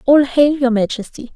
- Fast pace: No, average, 175 wpm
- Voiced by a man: No, female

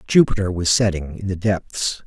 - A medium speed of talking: Yes, average, 175 wpm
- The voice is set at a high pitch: No, very low, 95 Hz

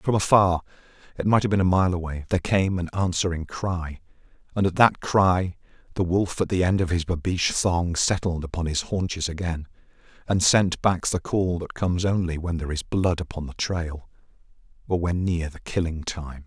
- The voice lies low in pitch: Yes, very low, 90 Hz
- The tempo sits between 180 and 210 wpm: Yes, average, 185 wpm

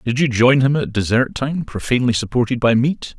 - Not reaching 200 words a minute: No, fast, 205 wpm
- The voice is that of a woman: No, male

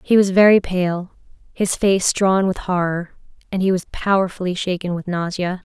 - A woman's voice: Yes, female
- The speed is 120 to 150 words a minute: No, average, 170 wpm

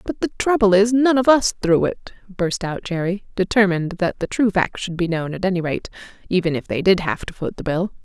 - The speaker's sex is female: Yes, female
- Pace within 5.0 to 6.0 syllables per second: Yes, 5.5 syllables/s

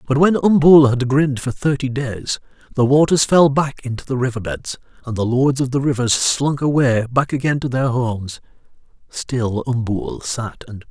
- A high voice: No, low, 130 Hz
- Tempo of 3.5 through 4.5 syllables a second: No, 5.0 syllables/s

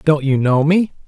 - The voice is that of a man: Yes, male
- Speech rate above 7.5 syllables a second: No, 4.7 syllables/s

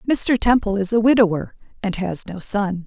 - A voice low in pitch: No, high, 205 Hz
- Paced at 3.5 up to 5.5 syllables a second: Yes, 5.1 syllables/s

